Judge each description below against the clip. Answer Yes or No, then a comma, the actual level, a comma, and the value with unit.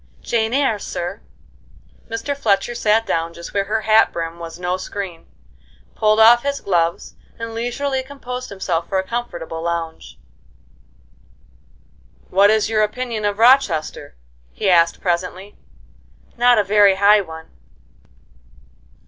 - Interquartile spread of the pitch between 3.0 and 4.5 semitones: No, average, 4.9 semitones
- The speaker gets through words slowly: Yes, slow, 130 wpm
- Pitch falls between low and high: No, high, 205 Hz